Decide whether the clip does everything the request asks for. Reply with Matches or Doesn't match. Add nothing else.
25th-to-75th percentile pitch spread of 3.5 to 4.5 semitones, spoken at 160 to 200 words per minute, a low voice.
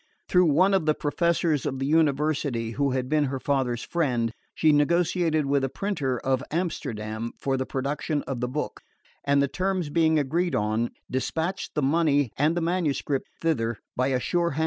Doesn't match